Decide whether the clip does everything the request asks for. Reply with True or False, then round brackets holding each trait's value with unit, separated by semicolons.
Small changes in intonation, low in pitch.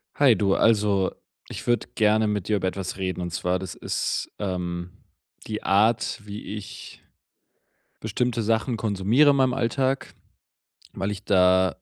False (3.4 semitones; 105 Hz)